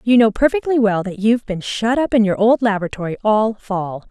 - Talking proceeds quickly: Yes, fast, 220 wpm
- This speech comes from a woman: Yes, female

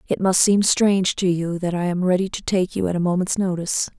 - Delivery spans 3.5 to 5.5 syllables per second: No, 5.8 syllables/s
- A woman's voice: Yes, female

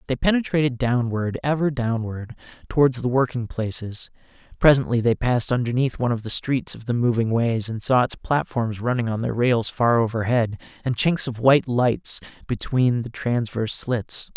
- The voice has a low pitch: Yes, low, 120 Hz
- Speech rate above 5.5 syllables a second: No, 5.0 syllables/s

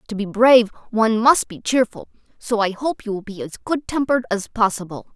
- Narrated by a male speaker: No, female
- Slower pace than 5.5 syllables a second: No, 5.7 syllables/s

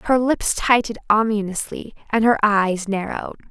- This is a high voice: Yes, high, 215 Hz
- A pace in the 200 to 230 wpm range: No, slow, 135 wpm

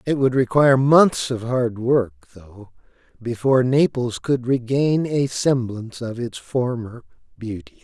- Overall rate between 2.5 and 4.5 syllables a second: Yes, 4.2 syllables/s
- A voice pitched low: Yes, low, 125 Hz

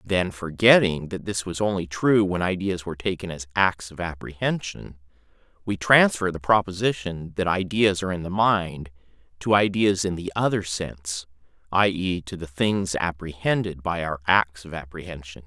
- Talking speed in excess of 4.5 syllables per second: Yes, 4.9 syllables/s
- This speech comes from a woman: No, male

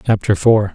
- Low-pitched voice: Yes, low, 105 Hz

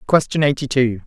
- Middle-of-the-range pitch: No, low, 130 Hz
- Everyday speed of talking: Yes, average, 170 wpm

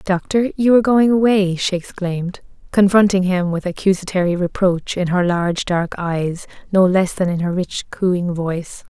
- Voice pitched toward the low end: No, medium, 185 Hz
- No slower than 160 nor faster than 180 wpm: Yes, average, 170 wpm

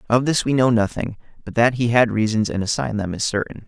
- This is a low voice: Yes, low, 115 Hz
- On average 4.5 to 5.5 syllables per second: No, 6.2 syllables/s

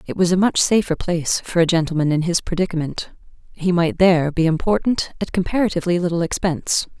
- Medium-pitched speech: Yes, medium, 175 Hz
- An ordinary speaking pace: Yes, average, 180 wpm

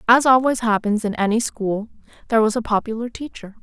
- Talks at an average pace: Yes, average, 180 wpm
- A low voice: No, high, 225 Hz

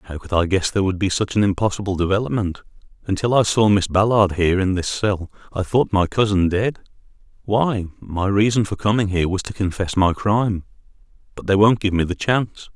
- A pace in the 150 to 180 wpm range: No, average, 200 wpm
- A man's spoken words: Yes, male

